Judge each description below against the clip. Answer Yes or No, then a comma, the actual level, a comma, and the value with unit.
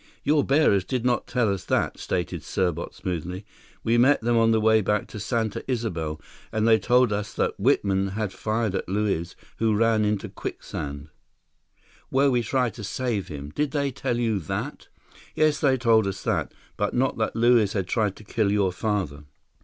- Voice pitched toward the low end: Yes, low, 110 Hz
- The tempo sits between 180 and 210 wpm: Yes, average, 185 wpm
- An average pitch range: Yes, average, 3.7 semitones